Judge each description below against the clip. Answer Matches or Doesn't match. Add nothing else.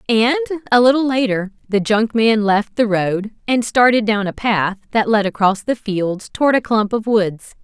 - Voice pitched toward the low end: Doesn't match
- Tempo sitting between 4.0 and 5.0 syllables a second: Matches